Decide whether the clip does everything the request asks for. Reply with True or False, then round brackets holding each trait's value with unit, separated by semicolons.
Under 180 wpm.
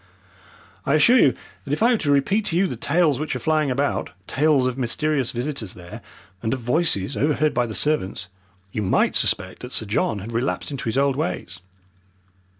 False (195 wpm)